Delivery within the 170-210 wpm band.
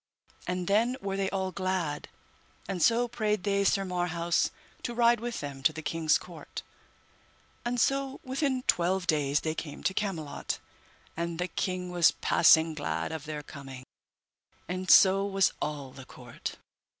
No: average, 155 wpm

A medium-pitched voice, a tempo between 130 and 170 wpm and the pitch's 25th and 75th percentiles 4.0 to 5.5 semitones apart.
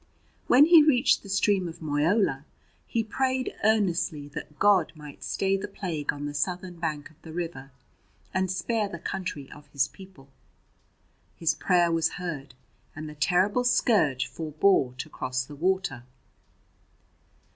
Yes: medium, 170 Hz; average, 145 wpm; average, 5.0 semitones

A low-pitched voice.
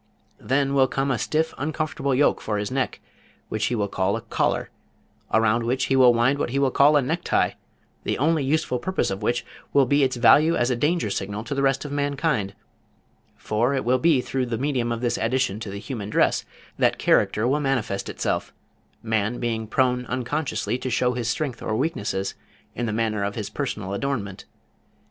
Yes: low, 125 Hz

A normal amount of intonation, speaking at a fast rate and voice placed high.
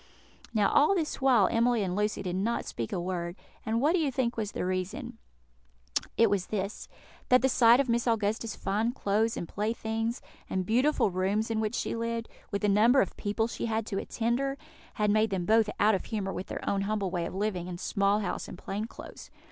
Yes: average, 3.0 semitones; fast, 215 wpm; high, 215 Hz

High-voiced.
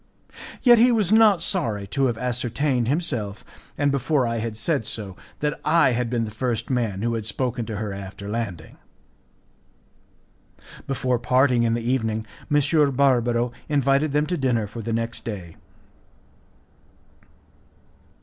No: low, 120 Hz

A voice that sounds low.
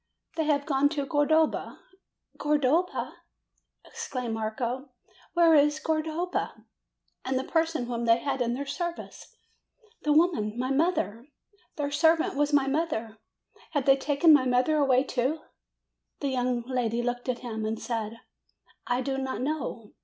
No: very high, 270 Hz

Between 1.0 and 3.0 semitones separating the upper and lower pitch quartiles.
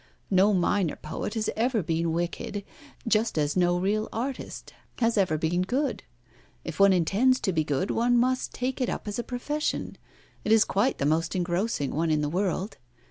No: wide, 5.6 semitones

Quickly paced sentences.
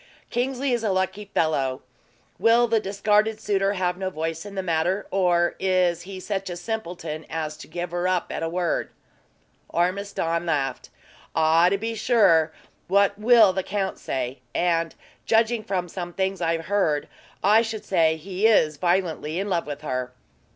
No: average, 165 wpm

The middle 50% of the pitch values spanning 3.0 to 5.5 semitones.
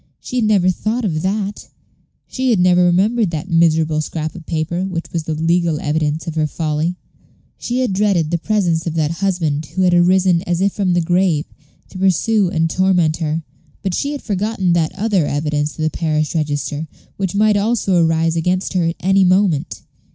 Yes: average, 3.3 semitones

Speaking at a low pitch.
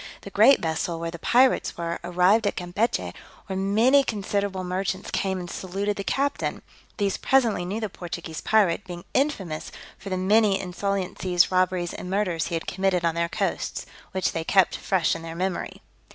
No: high, 190 Hz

